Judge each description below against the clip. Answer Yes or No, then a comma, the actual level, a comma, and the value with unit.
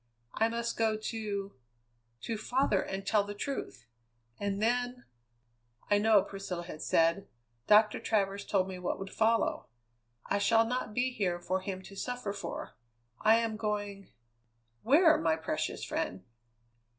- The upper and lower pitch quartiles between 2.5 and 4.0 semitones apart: Yes, average, 3.2 semitones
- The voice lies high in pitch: Yes, high, 205 Hz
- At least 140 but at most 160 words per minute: Yes, average, 150 wpm